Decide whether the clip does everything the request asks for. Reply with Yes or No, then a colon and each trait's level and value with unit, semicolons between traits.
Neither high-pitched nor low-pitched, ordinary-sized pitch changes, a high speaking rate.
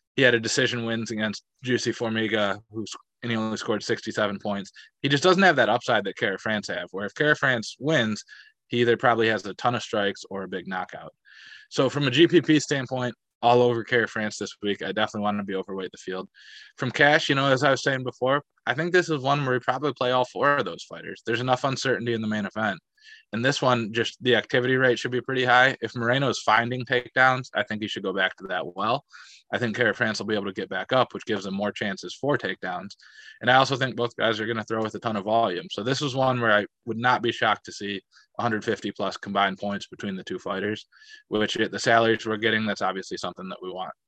No: low, 120 Hz; average, 3.4 semitones; fast, 245 wpm